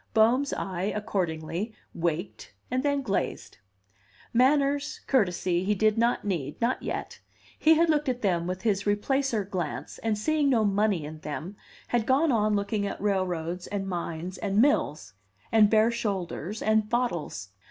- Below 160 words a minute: Yes, average, 150 wpm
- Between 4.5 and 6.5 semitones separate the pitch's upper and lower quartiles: Yes, average, 4.9 semitones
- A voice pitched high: Yes, high, 210 Hz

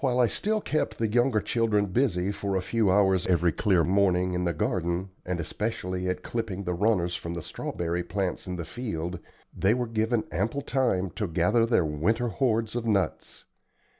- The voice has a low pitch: Yes, low, 100 Hz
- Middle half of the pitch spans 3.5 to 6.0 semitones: Yes, average, 4.2 semitones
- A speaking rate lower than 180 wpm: No, average, 185 wpm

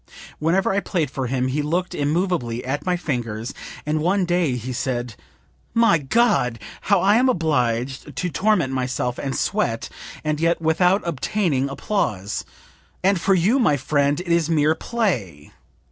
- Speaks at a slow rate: No, average, 155 wpm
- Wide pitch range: Yes, wide, 5.9 semitones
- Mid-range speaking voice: Yes, medium, 155 Hz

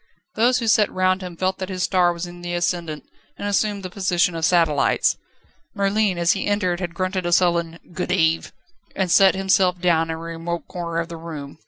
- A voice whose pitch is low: No, medium, 180 Hz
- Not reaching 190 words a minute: No, fast, 205 wpm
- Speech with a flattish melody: Yes, narrow, 2.0 semitones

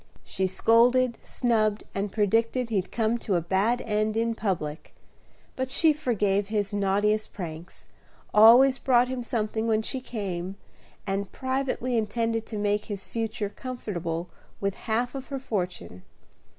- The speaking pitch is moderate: No, high, 220 Hz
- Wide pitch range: No, average, 3.3 semitones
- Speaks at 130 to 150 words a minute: Yes, average, 140 wpm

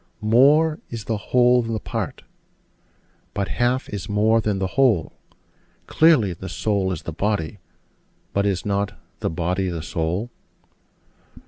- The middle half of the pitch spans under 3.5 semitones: No, average, 4.2 semitones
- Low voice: Yes, low, 105 Hz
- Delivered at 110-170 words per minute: Yes, average, 140 wpm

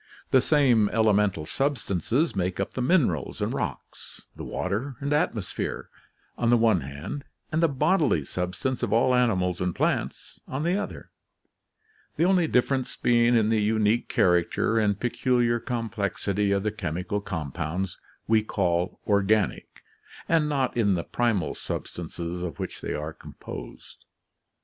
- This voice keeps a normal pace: Yes, average, 145 wpm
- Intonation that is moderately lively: No, wide, 5.8 semitones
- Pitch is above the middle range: No, low, 110 Hz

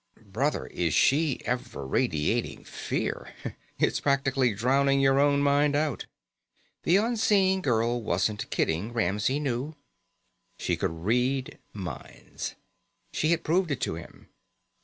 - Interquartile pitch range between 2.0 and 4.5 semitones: No, average, 5.3 semitones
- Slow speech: Yes, slow, 120 wpm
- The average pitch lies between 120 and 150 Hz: Yes, low, 135 Hz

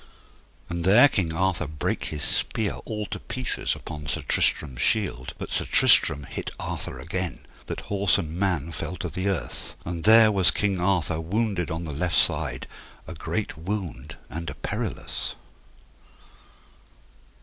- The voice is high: No, very low, 85 Hz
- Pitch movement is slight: No, average, 3.9 semitones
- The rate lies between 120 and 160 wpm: Yes, average, 150 wpm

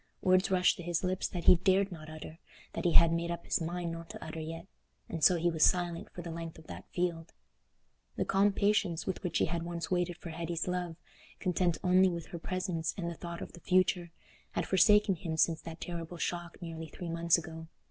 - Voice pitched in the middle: Yes, medium, 170 Hz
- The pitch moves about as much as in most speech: No, narrow, 1.6 semitones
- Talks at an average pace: No, fast, 215 wpm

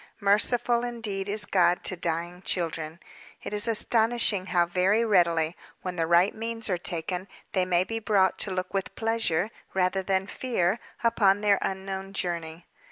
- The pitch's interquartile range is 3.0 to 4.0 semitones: Yes, average, 3.3 semitones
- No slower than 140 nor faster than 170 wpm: Yes, average, 160 wpm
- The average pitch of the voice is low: No, high, 190 Hz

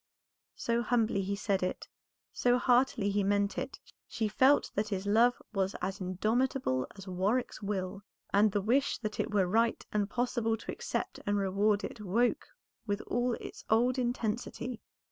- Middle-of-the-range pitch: No, high, 215 Hz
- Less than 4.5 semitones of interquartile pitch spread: Yes, average, 3.3 semitones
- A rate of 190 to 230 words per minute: No, average, 165 wpm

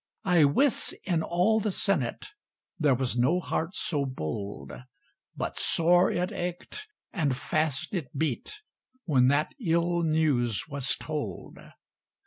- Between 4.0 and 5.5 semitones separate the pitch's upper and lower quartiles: Yes, average, 5.1 semitones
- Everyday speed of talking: No, slow, 125 wpm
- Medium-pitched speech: Yes, medium, 155 Hz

